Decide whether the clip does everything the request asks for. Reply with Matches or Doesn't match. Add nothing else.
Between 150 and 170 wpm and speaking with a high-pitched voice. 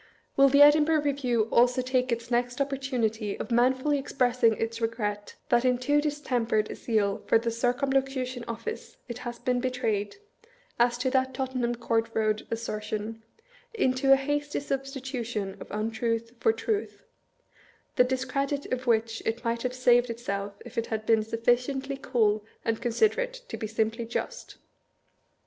Matches